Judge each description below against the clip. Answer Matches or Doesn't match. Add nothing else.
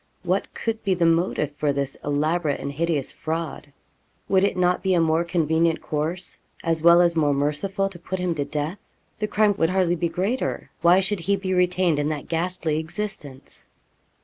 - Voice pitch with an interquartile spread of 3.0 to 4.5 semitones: Matches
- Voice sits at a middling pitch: Matches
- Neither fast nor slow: Matches